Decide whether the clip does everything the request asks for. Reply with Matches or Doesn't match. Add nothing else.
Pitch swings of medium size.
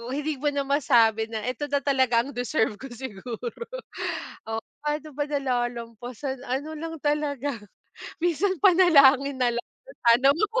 Matches